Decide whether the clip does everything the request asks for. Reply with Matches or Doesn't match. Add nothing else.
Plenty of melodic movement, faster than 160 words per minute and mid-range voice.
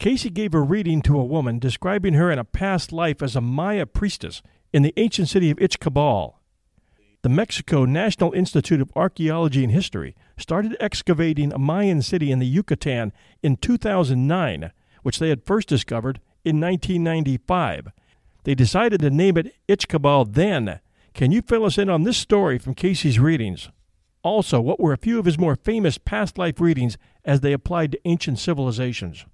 Matches